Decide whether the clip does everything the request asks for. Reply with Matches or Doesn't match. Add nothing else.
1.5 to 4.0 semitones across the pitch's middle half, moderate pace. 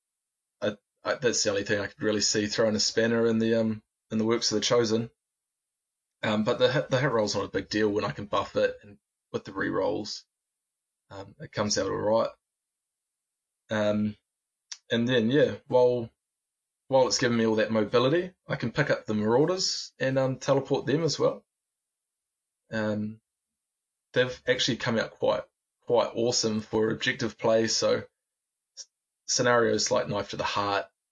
Matches